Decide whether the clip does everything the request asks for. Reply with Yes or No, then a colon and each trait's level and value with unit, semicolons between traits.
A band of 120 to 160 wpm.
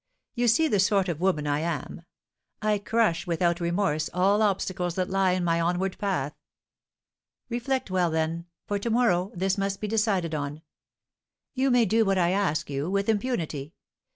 No: average, 170 wpm